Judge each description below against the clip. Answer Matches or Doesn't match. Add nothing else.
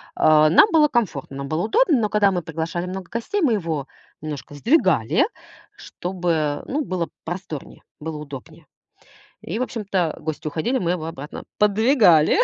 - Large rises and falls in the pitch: Matches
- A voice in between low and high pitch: Matches